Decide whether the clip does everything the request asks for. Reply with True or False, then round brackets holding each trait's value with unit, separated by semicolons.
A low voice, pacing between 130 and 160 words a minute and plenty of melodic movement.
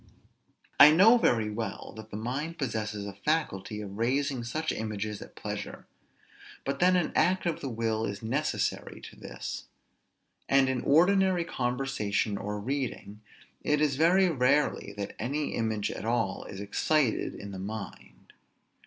True (120 Hz; 150 wpm; 6.1 semitones)